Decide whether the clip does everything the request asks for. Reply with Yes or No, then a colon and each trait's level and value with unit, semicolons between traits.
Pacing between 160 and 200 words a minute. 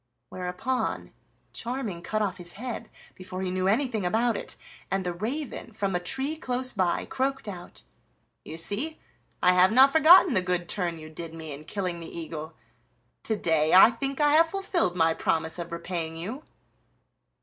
Yes: average, 170 wpm